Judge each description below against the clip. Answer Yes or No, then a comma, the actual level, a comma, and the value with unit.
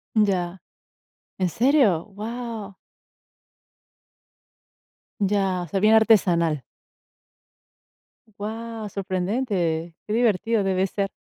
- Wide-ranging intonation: No, average, 3.3 semitones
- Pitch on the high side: Yes, high, 200 Hz